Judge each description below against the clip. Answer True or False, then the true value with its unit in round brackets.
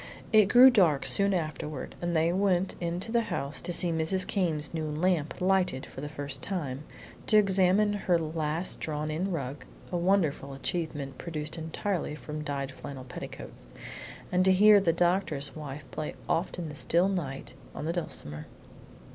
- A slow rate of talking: False (165 wpm)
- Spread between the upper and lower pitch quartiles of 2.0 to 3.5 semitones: False (3.9 semitones)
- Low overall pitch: False (165 Hz)